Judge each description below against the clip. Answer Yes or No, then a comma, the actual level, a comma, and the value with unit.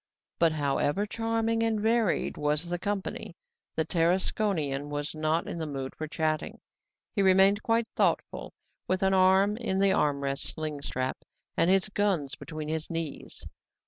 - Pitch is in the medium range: Yes, medium, 170 Hz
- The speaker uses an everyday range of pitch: Yes, average, 4.9 semitones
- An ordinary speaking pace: Yes, average, 155 wpm